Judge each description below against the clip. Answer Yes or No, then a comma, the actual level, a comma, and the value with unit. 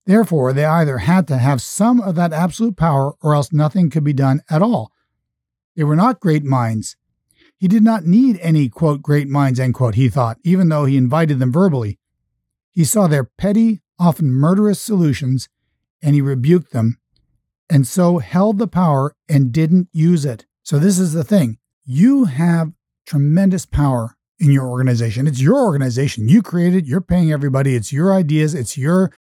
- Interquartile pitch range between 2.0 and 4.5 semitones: No, average, 5.1 semitones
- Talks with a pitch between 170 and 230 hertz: No, medium, 155 Hz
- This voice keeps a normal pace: Yes, average, 180 wpm